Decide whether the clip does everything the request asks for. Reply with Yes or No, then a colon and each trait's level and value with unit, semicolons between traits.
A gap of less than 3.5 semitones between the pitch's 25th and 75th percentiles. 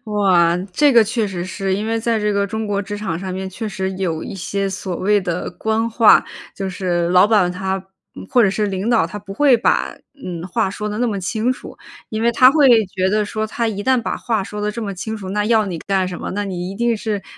Yes: average, 2.8 semitones